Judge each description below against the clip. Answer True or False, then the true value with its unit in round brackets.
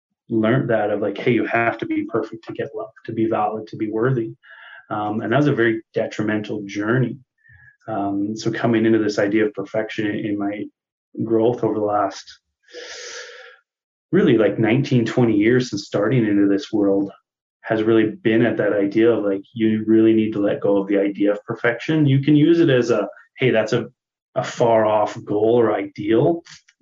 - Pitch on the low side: True (110 Hz)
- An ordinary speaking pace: True (190 wpm)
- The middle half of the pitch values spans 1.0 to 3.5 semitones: True (2.4 semitones)